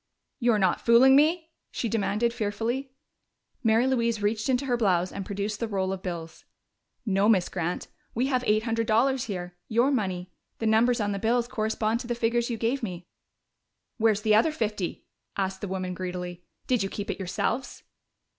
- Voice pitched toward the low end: No, high, 220 Hz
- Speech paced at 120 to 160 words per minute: No, average, 180 wpm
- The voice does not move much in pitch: No, average, 3.7 semitones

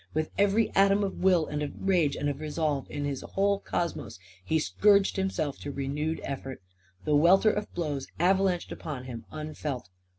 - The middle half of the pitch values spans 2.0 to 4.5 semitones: No, average, 5.1 semitones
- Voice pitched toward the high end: No, medium, 155 Hz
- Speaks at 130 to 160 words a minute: No, average, 170 wpm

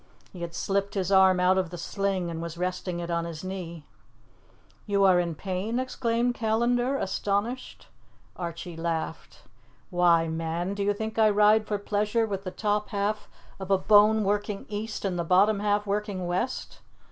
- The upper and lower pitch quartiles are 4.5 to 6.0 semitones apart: No, average, 3.0 semitones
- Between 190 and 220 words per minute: No, average, 170 wpm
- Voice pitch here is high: Yes, high, 195 Hz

